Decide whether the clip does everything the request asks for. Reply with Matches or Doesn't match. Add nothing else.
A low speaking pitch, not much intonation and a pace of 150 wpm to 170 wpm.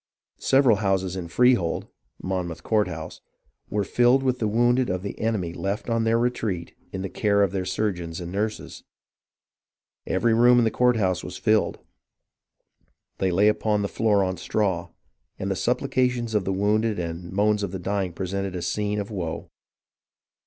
Doesn't match